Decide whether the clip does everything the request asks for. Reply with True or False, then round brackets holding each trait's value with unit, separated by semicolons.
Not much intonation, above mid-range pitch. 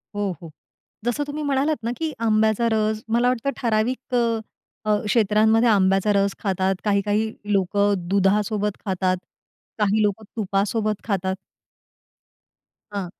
True (2.3 semitones; 210 Hz)